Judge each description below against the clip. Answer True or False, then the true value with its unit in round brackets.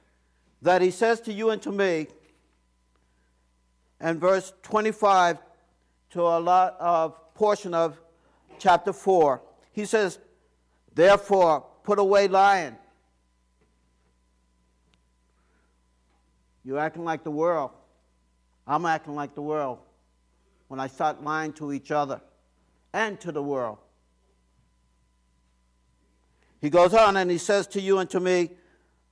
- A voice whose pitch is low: False (145 Hz)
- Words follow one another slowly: True (115 wpm)